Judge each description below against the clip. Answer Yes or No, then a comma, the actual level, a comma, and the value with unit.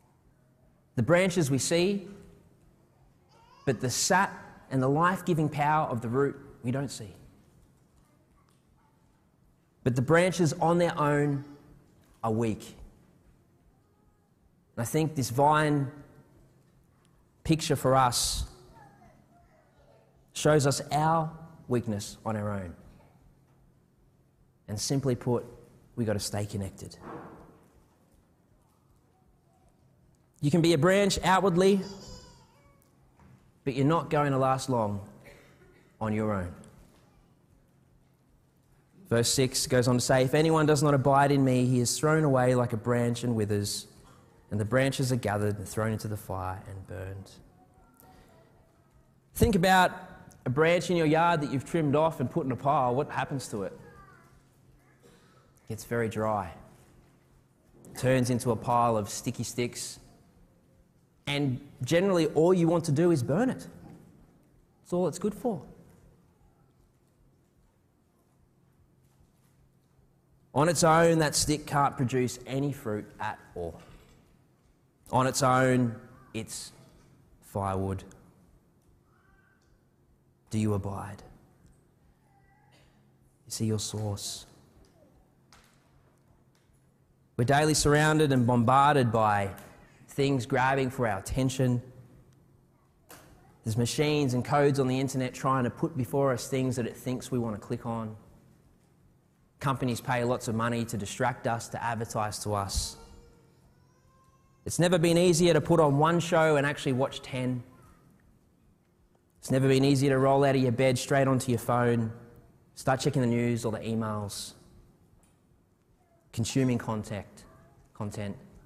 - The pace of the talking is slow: Yes, slow, 125 wpm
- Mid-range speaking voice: No, low, 130 Hz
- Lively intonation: No, average, 4.6 semitones